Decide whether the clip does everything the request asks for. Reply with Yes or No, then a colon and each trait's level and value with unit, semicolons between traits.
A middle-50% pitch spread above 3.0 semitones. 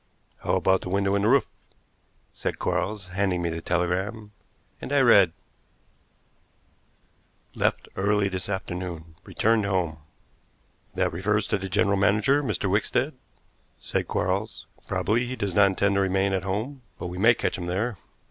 No: narrow, 2.5 semitones